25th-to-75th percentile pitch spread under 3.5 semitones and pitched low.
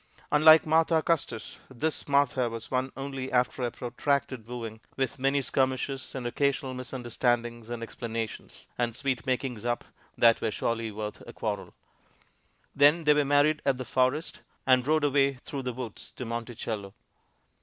Yes: average, 2.9 semitones; low, 130 Hz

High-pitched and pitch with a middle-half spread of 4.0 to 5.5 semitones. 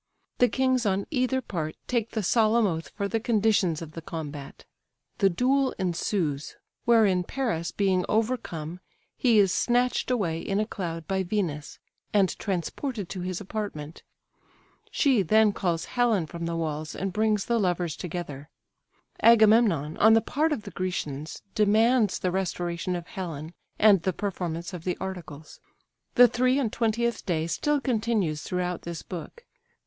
Yes: high, 195 Hz; average, 5.0 semitones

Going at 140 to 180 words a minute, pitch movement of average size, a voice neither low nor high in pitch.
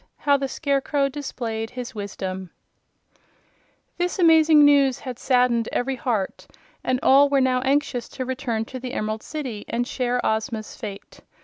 No: average, 145 wpm; average, 3.7 semitones; very high, 255 Hz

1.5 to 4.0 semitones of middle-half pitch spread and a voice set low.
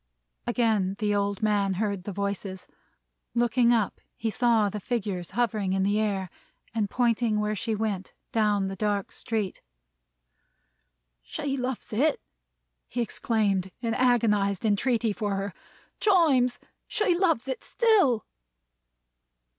No: average, 3.3 semitones; high, 215 Hz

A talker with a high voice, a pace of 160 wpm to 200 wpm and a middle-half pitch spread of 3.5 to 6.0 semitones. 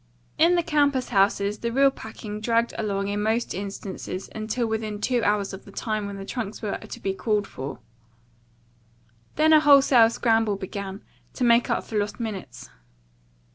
No: high, 215 Hz; average, 170 wpm; average, 3.0 semitones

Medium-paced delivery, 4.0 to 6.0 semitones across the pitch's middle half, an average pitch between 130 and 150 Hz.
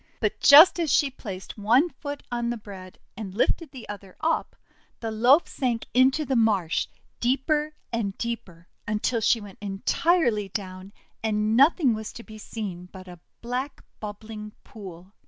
No: average, 160 wpm; average, 4.7 semitones; high, 225 Hz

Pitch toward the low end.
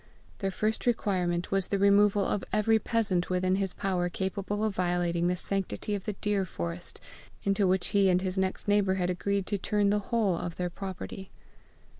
No: high, 195 Hz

